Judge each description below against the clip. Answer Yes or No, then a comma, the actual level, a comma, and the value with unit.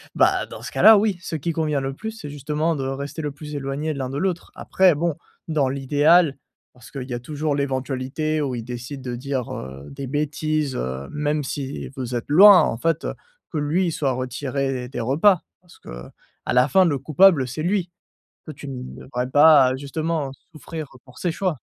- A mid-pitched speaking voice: Yes, medium, 145 Hz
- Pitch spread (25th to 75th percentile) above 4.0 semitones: No, average, 3.4 semitones